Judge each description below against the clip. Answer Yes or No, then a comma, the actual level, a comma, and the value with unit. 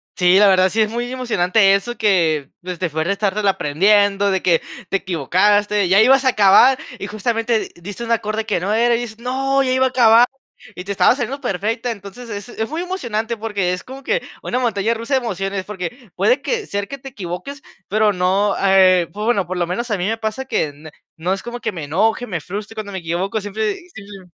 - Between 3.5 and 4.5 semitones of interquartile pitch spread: Yes, average, 4.1 semitones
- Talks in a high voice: Yes, high, 210 Hz